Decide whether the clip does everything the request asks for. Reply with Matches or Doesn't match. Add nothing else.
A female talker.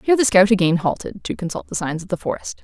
Matches